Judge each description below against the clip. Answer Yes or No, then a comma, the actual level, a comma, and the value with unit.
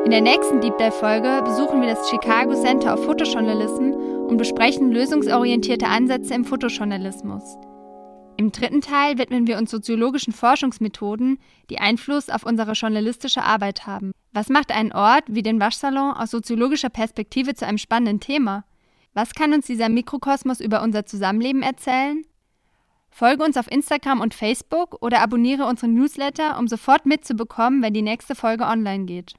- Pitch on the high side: Yes, high, 235 Hz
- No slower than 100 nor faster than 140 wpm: No, average, 155 wpm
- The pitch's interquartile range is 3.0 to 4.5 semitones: Yes, average, 3.7 semitones